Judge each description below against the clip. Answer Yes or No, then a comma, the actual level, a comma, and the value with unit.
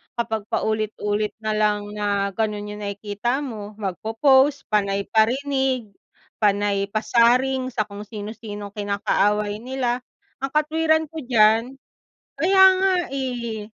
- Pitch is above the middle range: Yes, high, 220 Hz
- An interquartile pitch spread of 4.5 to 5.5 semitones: No, average, 3.9 semitones